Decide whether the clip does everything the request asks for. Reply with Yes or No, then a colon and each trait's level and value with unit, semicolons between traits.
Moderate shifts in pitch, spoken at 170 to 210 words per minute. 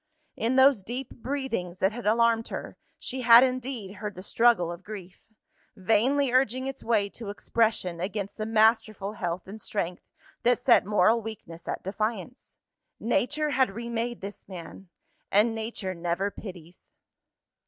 No: average, 3.9 semitones; average, 145 wpm